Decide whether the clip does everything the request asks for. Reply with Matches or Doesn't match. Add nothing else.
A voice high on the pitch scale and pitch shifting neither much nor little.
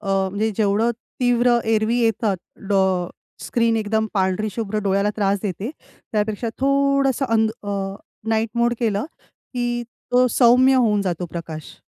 Matches